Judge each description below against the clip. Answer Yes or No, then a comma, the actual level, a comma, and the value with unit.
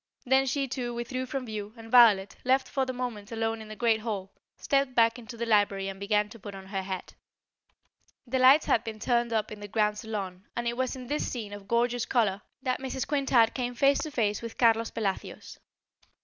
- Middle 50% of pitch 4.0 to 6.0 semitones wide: No, average, 3.3 semitones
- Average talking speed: No, fast, 215 wpm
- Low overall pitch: No, high, 230 Hz